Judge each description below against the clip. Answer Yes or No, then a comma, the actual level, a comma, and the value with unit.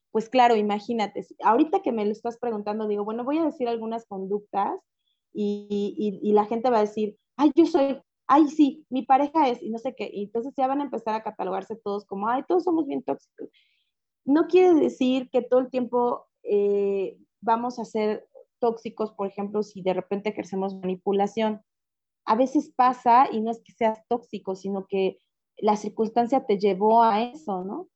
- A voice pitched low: No, high, 230 Hz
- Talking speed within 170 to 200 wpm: Yes, fast, 190 wpm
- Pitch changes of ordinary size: Yes, average, 4.1 semitones